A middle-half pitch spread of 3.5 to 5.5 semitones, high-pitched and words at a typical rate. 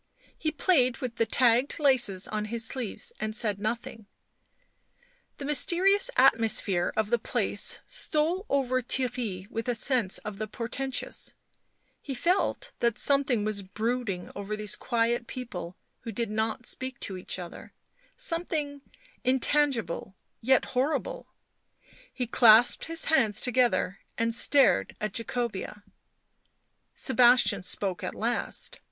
No: average, 4.0 semitones; high, 240 Hz; slow, 130 wpm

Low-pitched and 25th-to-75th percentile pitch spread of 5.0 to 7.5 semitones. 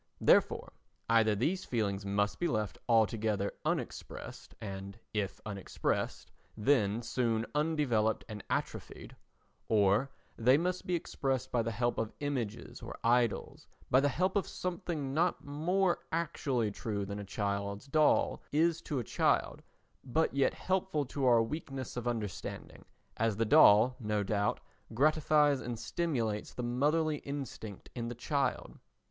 Yes: low, 120 Hz; wide, 5.6 semitones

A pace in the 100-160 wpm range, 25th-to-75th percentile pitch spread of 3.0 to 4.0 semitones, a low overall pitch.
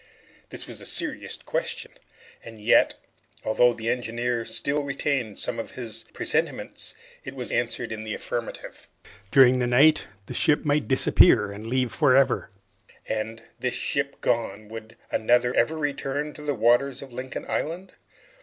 Yes: average, 155 wpm; average, 3.6 semitones; low, 125 Hz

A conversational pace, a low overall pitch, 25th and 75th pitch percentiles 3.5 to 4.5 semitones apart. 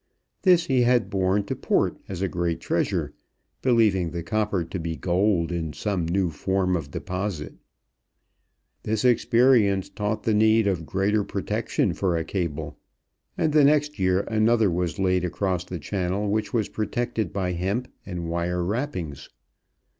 Yes: average, 155 wpm; very low, 95 Hz; average, 3.9 semitones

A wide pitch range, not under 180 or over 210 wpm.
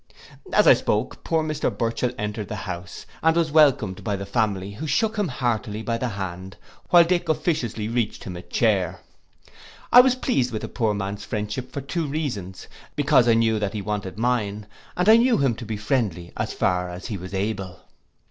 Yes: wide, 6.3 semitones; average, 200 wpm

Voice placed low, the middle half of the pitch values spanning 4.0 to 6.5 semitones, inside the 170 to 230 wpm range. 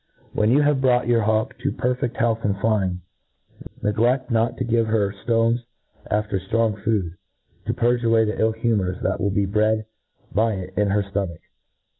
No: low, 110 Hz; narrow, 2.6 semitones; average, 185 wpm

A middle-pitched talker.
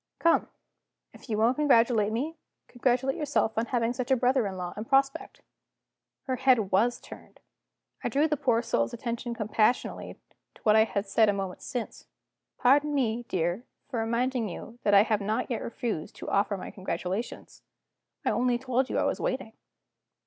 No: high, 235 Hz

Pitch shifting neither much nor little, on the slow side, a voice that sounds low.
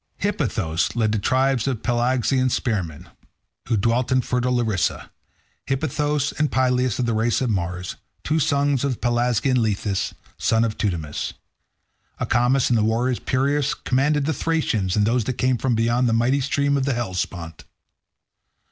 No: average, 3.4 semitones; average, 155 wpm; low, 120 Hz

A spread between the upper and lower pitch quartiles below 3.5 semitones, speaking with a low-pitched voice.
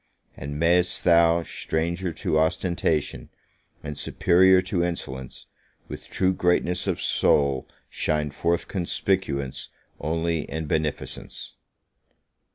Yes: average, 2.7 semitones; very low, 85 Hz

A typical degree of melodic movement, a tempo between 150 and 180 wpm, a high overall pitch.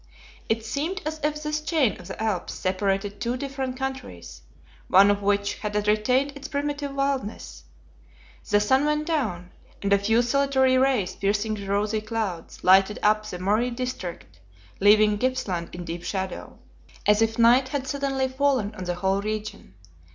Yes: average, 5.0 semitones; average, 160 wpm; high, 215 Hz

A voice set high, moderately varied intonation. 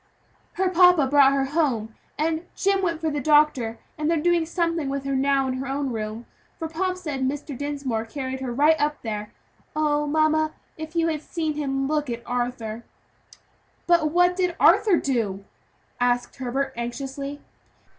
Yes: very high, 290 Hz; average, 3.6 semitones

